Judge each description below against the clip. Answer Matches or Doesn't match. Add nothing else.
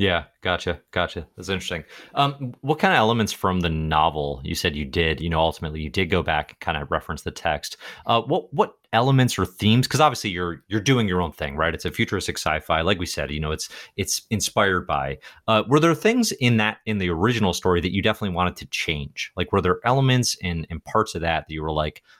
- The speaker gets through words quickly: Matches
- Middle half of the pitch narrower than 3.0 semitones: Doesn't match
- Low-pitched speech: Matches